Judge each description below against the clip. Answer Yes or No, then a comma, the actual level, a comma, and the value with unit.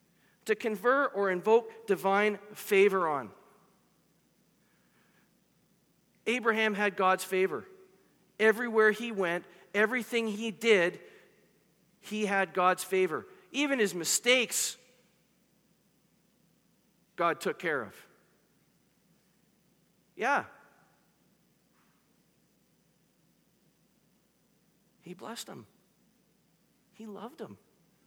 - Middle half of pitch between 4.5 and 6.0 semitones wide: No, average, 2.9 semitones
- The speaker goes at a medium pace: No, slow, 75 wpm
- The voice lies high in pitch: Yes, high, 210 Hz